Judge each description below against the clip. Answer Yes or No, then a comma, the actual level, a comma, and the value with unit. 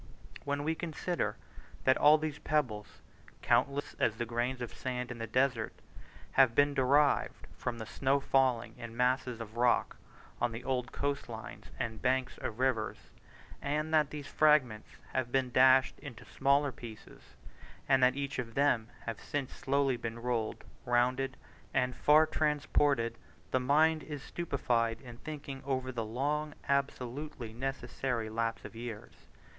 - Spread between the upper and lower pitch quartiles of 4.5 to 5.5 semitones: No, average, 3.2 semitones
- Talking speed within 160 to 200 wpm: No, average, 150 wpm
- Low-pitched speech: Yes, low, 130 Hz